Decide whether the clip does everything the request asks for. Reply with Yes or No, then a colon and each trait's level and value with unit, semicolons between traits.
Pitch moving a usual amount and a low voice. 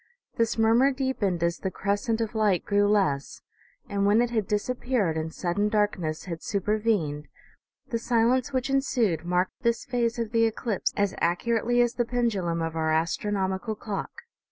No: average, 4.3 semitones; high, 210 Hz